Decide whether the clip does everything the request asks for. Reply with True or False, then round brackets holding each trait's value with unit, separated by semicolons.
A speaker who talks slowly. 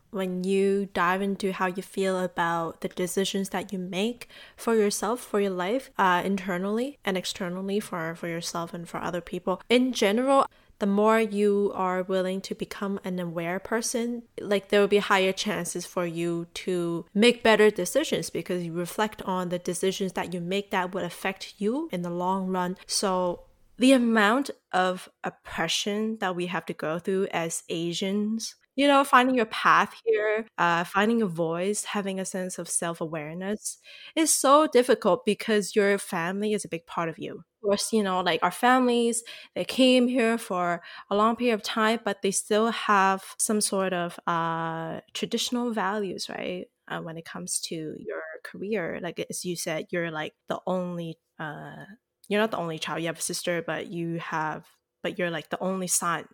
False (180 wpm)